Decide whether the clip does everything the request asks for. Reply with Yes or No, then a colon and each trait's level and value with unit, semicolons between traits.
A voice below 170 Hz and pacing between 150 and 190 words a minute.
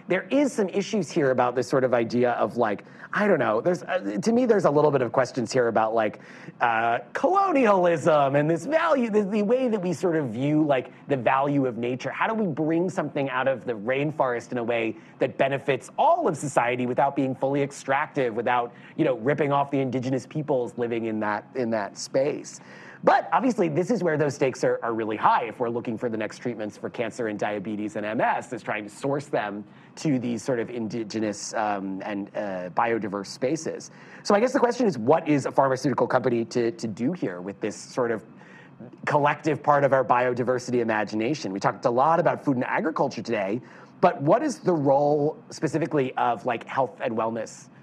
No: low, 135 Hz; fast, 205 wpm